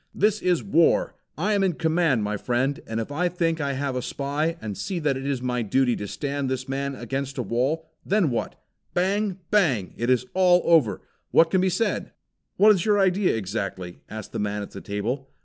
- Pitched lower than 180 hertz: Yes, medium, 140 Hz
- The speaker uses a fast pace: Yes, fast, 215 wpm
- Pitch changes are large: Yes, wide, 6.6 semitones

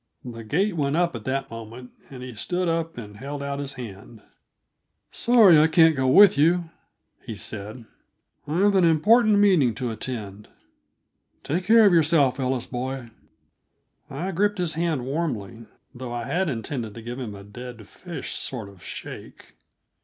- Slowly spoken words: No, average, 165 wpm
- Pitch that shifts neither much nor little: No, wide, 6.3 semitones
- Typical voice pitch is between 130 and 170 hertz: Yes, low, 135 Hz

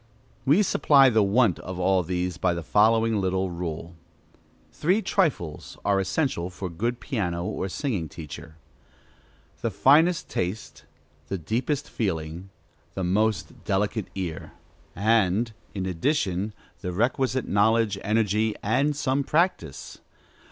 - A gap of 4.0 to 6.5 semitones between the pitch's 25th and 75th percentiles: Yes, average, 5.2 semitones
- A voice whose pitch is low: Yes, low, 100 Hz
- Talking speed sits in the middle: No, slow, 125 wpm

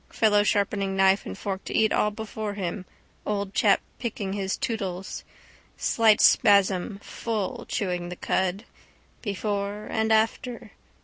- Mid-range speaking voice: No, high, 205 Hz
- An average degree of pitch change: No, narrow, 2.1 semitones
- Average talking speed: No, slow, 130 wpm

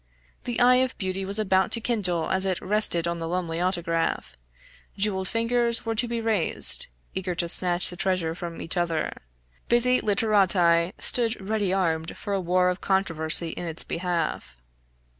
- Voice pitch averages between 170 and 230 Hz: Yes, medium, 185 Hz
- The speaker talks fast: No, average, 165 wpm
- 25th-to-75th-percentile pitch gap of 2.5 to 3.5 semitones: No, average, 3.9 semitones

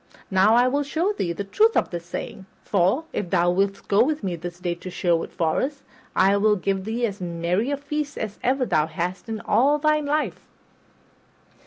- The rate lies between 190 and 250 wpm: Yes, average, 195 wpm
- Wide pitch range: Yes, wide, 7.5 semitones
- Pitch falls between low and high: No, high, 200 Hz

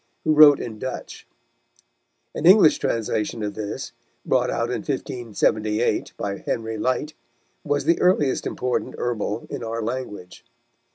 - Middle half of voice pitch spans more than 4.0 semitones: Yes, average, 5.1 semitones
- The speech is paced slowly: Yes, slow, 130 wpm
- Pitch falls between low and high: No, low, 120 Hz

